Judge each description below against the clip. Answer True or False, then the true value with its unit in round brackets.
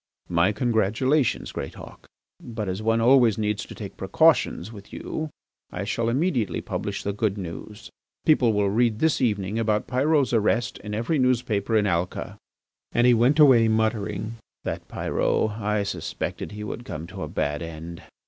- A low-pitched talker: True (110 Hz)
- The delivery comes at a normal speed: True (165 wpm)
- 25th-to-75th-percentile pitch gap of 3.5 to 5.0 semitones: False (3.1 semitones)